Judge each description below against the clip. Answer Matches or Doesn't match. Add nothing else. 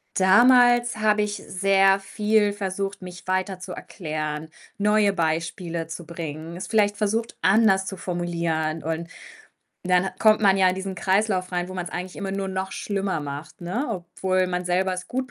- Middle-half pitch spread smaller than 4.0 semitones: Matches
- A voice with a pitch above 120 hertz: Matches